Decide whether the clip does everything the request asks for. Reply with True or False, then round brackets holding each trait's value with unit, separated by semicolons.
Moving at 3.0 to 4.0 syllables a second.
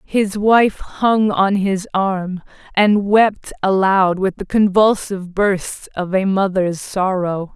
True (3.3 syllables/s)